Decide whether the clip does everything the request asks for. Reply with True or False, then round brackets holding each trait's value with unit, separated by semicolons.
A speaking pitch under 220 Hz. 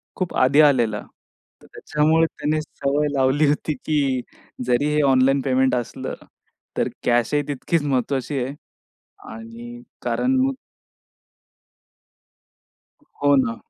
True (140 Hz)